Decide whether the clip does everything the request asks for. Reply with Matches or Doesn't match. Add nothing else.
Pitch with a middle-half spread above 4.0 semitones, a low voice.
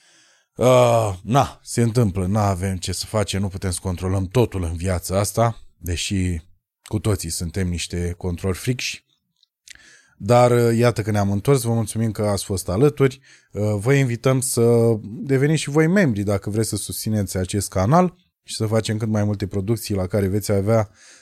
Doesn't match